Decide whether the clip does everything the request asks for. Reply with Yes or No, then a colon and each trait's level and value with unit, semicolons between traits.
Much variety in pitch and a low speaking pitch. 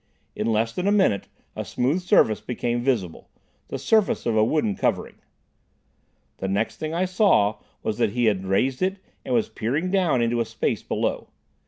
Yes: wide, 8.4 semitones; low, 120 Hz